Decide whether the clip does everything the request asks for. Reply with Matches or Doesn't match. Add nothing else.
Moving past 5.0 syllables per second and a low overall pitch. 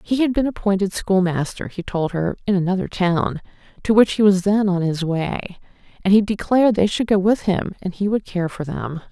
Doesn't match